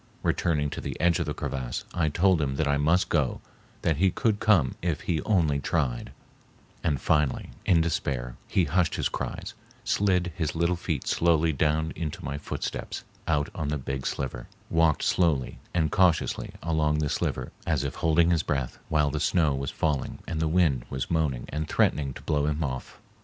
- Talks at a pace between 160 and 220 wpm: Yes, average, 185 wpm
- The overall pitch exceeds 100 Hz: No, very low, 75 Hz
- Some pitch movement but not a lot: Yes, average, 3.1 semitones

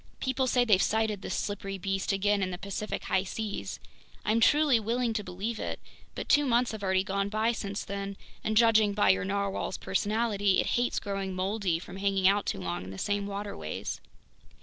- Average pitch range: No, narrow, 2.3 semitones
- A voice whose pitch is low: No, high, 200 Hz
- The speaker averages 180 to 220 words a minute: Yes, average, 190 wpm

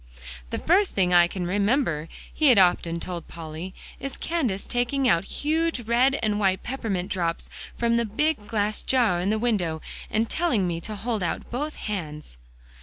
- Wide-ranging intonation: Yes, wide, 5.8 semitones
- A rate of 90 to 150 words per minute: No, average, 175 wpm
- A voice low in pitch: No, high, 210 Hz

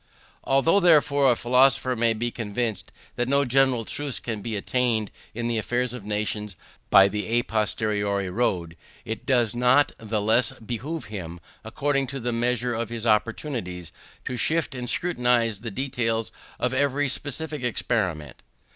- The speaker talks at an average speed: Yes, average, 150 wpm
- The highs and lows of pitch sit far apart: No, average, 3.4 semitones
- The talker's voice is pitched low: Yes, low, 120 Hz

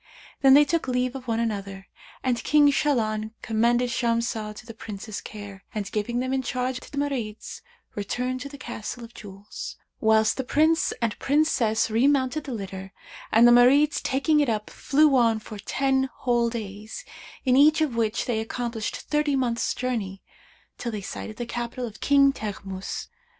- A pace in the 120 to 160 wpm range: No, average, 170 wpm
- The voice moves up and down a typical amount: Yes, average, 3.7 semitones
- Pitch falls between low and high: No, high, 240 Hz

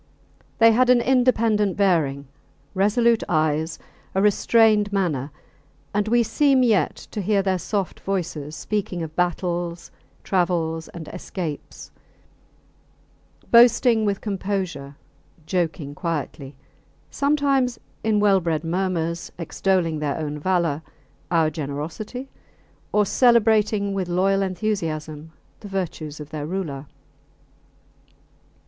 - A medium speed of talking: No, slow, 105 wpm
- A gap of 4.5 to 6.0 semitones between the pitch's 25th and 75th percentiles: Yes, average, 4.8 semitones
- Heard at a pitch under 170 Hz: No, medium, 185 Hz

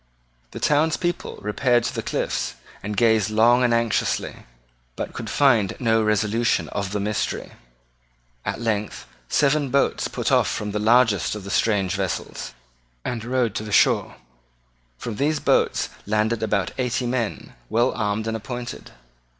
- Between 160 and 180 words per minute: No, average, 150 wpm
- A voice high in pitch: No, low, 110 Hz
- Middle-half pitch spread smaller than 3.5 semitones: Yes, average, 2.7 semitones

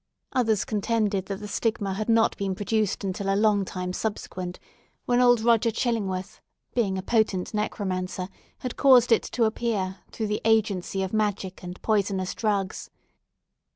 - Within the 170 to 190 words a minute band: No, average, 155 wpm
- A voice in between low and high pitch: No, high, 205 Hz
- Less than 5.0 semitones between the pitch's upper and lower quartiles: Yes, average, 2.8 semitones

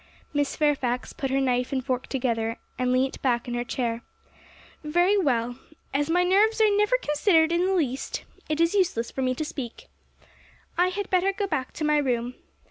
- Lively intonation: Yes, wide, 6.1 semitones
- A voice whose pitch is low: No, very high, 290 Hz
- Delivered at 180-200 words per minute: Yes, average, 190 wpm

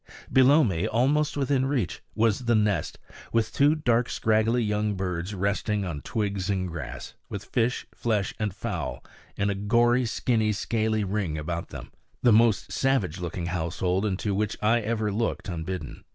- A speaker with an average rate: Yes, average, 160 wpm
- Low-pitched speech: Yes, low, 105 Hz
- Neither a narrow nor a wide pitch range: Yes, average, 4.0 semitones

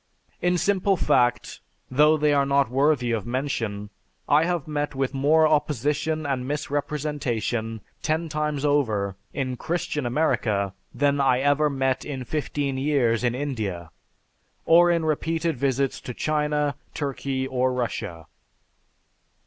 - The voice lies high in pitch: No, medium, 140 Hz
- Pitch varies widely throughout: No, average, 3.2 semitones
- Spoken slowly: Yes, slow, 130 wpm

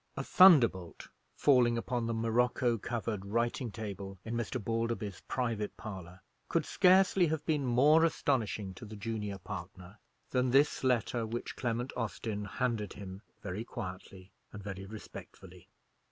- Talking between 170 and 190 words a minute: No, average, 140 wpm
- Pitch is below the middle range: Yes, low, 115 Hz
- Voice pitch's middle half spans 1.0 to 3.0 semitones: No, average, 3.7 semitones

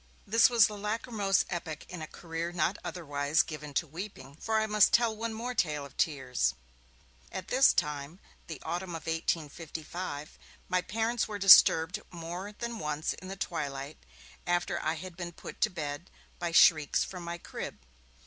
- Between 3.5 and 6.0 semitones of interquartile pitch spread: Yes, average, 4.8 semitones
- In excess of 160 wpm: Yes, average, 170 wpm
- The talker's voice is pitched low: No, medium, 175 Hz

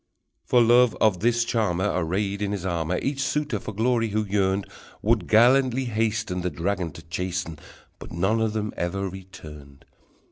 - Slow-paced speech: No, average, 165 wpm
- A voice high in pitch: No, low, 100 Hz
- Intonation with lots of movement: No, average, 4.0 semitones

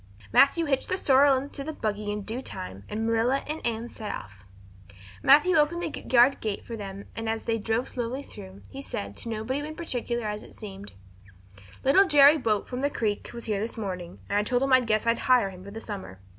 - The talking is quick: Yes, fast, 220 wpm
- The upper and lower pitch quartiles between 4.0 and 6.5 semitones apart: Yes, average, 4.7 semitones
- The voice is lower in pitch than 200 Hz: No, high, 230 Hz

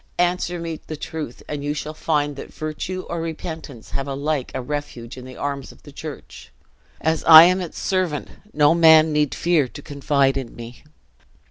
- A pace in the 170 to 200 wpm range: Yes, average, 180 wpm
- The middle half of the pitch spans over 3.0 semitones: No, average, 2.7 semitones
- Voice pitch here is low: No, medium, 150 Hz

